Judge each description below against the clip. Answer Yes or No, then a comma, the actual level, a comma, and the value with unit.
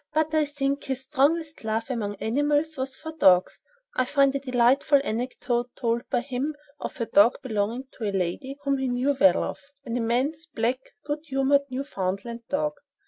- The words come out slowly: No, average, 175 wpm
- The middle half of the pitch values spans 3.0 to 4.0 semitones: Yes, average, 3.5 semitones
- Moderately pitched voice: No, very high, 260 Hz